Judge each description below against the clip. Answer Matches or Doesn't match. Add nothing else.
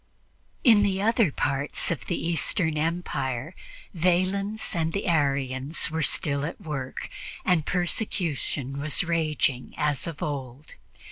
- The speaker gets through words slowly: Matches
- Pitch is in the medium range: Matches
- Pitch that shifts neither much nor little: Matches